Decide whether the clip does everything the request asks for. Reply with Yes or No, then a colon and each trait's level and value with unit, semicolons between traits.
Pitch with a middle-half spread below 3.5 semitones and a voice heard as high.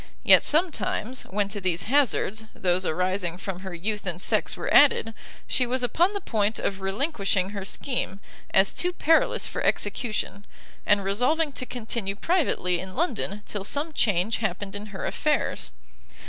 No: average, 5.2 semitones; high, 210 Hz